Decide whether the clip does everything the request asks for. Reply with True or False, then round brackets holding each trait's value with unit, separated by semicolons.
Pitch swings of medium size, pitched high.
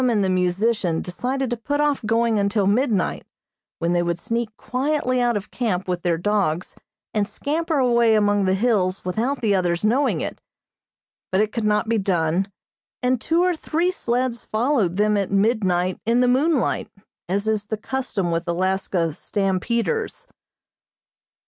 True (4.8 semitones; 215 Hz)